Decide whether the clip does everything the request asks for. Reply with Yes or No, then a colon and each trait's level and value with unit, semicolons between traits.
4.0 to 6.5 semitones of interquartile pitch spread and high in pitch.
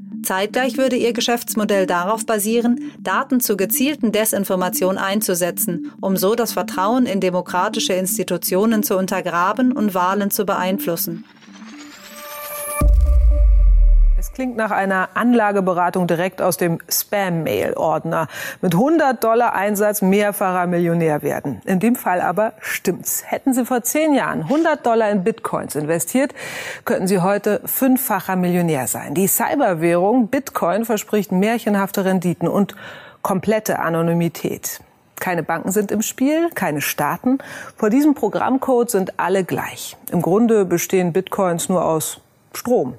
Yes: average, 4.3 semitones; high, 200 Hz